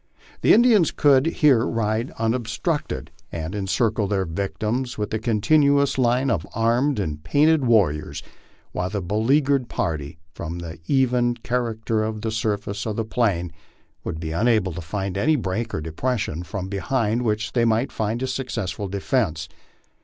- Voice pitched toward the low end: Yes, low, 110 Hz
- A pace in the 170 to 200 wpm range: No, average, 160 wpm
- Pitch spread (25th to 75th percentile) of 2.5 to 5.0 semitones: Yes, average, 4.6 semitones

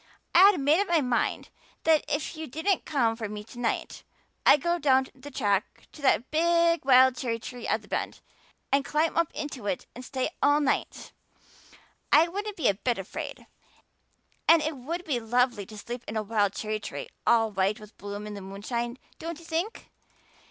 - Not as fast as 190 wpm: No, average, 195 wpm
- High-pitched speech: Yes, very high, 260 Hz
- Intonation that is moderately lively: No, wide, 6.3 semitones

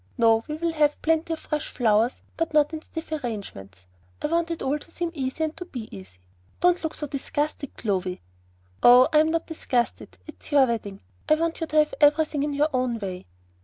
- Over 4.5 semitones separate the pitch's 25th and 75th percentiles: Yes, average, 5.3 semitones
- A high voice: Yes, very high, 295 Hz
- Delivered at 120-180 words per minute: No, average, 200 wpm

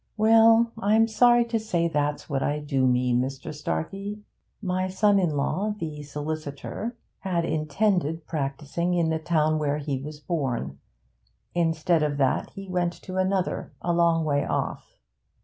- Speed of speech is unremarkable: Yes, average, 150 wpm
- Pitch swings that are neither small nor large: Yes, average, 4.6 semitones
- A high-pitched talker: No, medium, 165 Hz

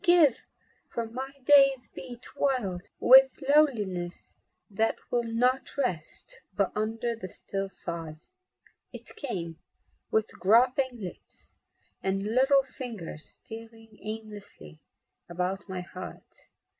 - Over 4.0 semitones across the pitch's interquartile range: Yes, wide, 5.4 semitones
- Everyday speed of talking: No, slow, 105 wpm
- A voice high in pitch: Yes, high, 225 Hz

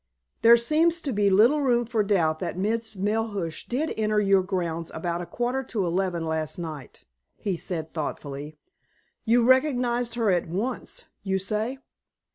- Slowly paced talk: No, average, 155 wpm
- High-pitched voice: Yes, high, 205 Hz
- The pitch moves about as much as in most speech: No, wide, 5.7 semitones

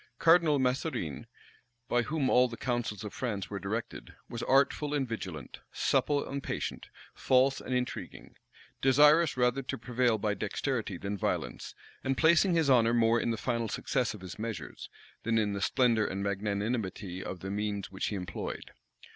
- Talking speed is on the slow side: No, average, 165 wpm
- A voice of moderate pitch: No, low, 115 Hz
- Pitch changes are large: No, average, 4.5 semitones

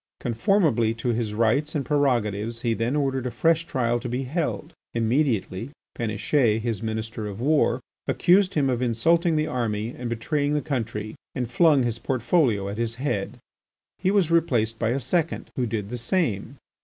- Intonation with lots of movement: No, average, 4.7 semitones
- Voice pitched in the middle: No, low, 120 Hz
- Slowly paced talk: No, average, 170 wpm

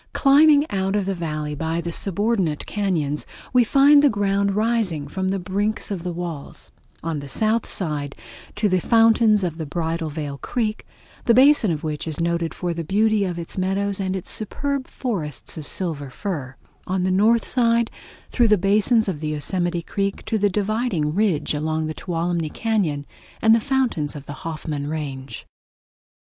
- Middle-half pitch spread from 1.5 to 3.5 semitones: No, wide, 5.4 semitones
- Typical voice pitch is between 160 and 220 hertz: Yes, medium, 185 Hz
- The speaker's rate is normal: Yes, average, 175 wpm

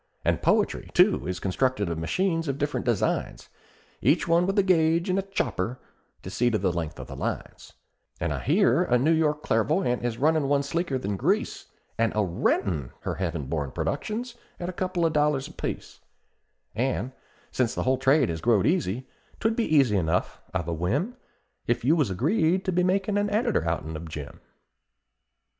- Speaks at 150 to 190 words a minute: Yes, average, 185 wpm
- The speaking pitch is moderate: No, low, 130 Hz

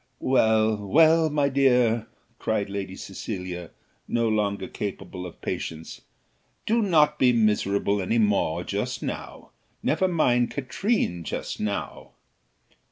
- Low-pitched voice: Yes, low, 110 Hz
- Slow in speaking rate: Yes, slow, 115 wpm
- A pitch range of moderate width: No, wide, 5.8 semitones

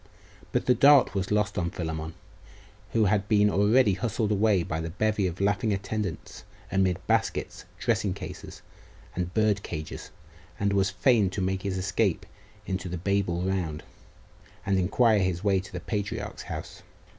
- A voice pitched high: No, very low, 95 Hz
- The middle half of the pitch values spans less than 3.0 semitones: Yes, narrow, 2.5 semitones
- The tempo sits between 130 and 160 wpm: Yes, average, 155 wpm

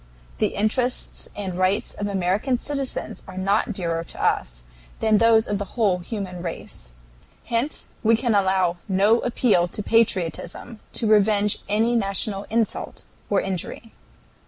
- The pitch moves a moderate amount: Yes, average, 3.4 semitones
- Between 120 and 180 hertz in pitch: No, high, 205 Hz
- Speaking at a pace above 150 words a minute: No, average, 140 wpm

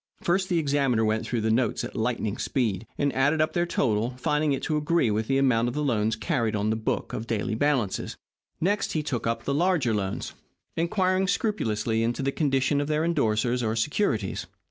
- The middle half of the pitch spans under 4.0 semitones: No, wide, 5.4 semitones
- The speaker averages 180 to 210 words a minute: Yes, average, 195 wpm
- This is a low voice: Yes, low, 130 Hz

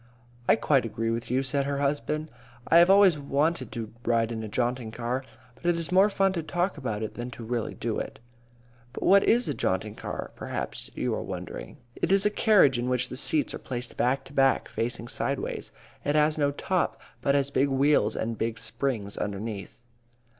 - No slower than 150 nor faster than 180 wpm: No, fast, 205 wpm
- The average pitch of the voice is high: No, low, 135 Hz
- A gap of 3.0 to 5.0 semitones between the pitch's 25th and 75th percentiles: Yes, average, 4.7 semitones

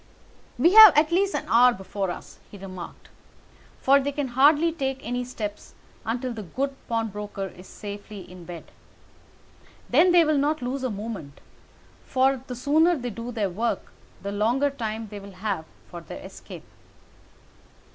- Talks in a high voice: Yes, high, 240 Hz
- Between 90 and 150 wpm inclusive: No, average, 160 wpm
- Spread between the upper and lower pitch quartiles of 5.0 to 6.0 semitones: Yes, wide, 5.5 semitones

